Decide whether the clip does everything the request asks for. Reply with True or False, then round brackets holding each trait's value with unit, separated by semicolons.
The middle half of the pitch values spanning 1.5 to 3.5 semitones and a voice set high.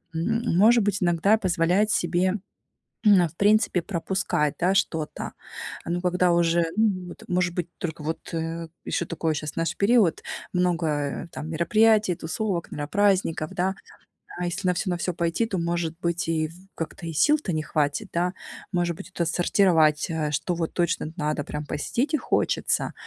False (2.7 semitones; 175 Hz)